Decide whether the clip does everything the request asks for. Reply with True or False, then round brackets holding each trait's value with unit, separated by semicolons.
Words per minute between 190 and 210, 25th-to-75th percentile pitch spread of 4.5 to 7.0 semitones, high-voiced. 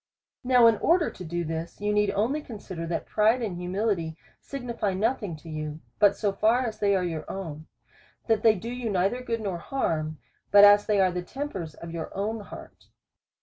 True (195 wpm; 4.8 semitones; 200 Hz)